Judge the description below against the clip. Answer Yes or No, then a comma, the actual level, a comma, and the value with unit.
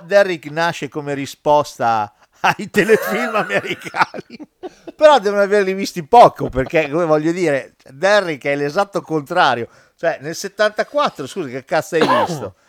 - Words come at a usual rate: Yes, average, 130 wpm